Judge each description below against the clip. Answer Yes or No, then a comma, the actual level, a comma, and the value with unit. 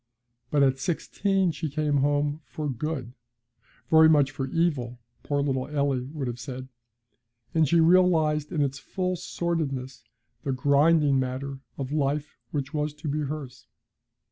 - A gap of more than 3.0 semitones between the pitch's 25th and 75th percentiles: No, average, 2.7 semitones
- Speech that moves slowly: No, average, 145 wpm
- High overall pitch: No, medium, 145 Hz